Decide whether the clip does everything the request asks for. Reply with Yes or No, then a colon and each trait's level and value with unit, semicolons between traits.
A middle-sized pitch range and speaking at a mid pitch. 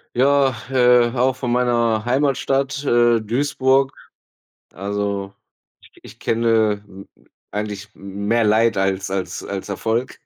No: average, 3.8 semitones; low, 115 Hz